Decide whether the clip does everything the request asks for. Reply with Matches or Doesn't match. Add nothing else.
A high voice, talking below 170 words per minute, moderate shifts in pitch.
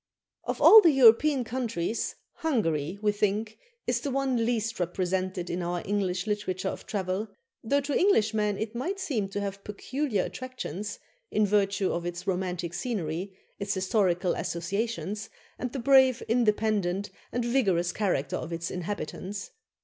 Matches